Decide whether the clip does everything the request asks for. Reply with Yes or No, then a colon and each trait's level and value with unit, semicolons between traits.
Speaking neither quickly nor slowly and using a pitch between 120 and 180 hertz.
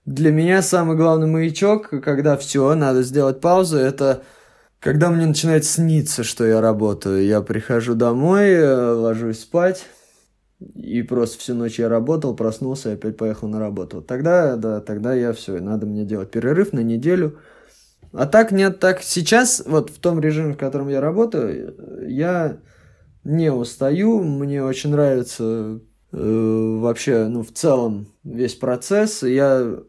Yes: average, 150 wpm; low, 130 Hz